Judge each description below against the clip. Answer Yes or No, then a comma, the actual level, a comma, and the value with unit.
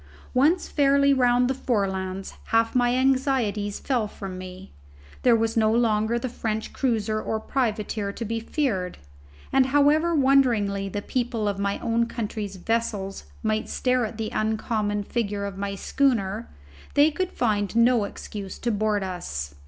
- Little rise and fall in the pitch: No, average, 3.7 semitones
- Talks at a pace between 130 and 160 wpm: Yes, average, 150 wpm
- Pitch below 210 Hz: No, high, 220 Hz